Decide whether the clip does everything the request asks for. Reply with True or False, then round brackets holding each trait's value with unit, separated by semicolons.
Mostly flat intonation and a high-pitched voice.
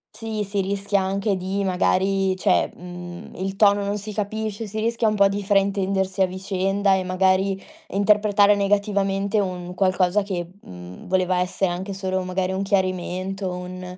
True (1.5 semitones; 195 Hz)